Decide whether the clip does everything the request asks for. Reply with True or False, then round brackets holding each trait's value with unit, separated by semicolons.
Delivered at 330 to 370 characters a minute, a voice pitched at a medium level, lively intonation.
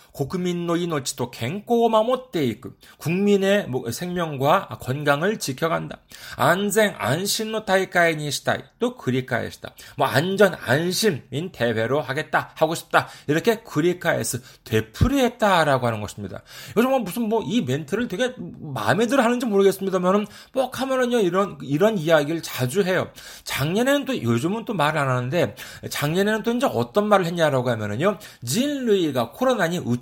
True (340 characters per minute; 175 Hz; 8.1 semitones)